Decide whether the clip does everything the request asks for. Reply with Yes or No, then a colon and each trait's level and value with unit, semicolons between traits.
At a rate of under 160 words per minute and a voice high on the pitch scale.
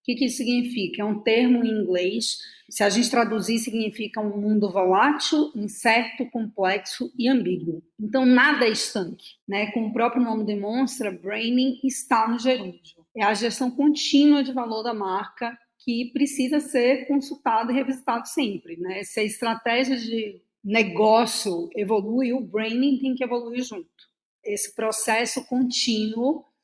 Yes: average, 150 wpm; high, 235 Hz